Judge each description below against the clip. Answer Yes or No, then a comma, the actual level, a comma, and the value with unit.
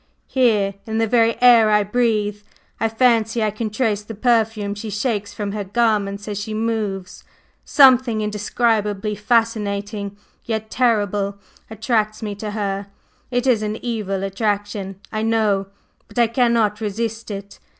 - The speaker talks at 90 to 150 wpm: Yes, average, 145 wpm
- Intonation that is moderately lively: No, narrow, 1.9 semitones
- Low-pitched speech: No, high, 215 Hz